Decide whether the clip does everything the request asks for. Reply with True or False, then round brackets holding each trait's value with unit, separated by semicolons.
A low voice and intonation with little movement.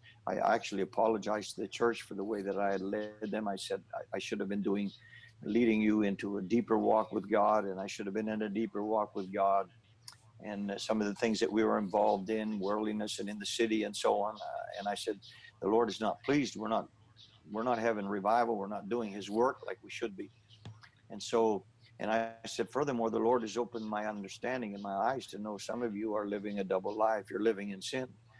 True (105 Hz; 1.9 semitones)